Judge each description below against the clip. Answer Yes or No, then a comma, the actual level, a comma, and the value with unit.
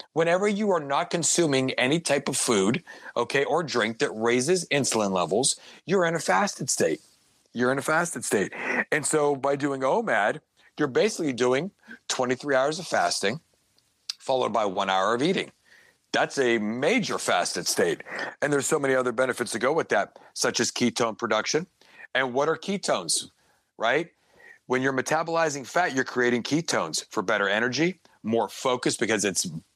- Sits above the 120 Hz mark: Yes, medium, 140 Hz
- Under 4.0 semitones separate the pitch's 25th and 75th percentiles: No, average, 4.6 semitones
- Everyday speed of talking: Yes, average, 165 wpm